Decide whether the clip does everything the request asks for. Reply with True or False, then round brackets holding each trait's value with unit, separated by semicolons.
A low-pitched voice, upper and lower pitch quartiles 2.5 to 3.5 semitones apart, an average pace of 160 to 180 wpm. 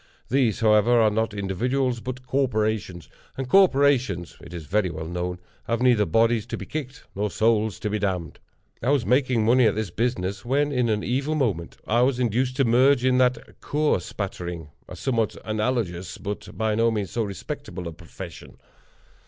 False (115 Hz; 4.3 semitones; 175 wpm)